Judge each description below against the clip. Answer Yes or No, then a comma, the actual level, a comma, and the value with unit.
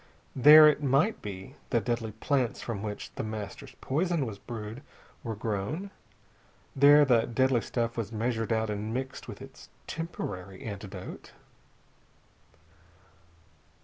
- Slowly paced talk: Yes, slow, 125 wpm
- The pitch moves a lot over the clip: No, average, 4.3 semitones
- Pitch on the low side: Yes, low, 115 Hz